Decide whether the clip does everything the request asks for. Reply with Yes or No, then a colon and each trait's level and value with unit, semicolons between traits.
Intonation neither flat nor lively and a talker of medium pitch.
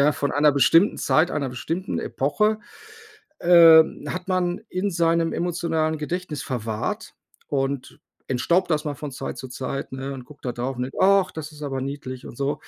Yes: average, 4.2 semitones; medium, 150 Hz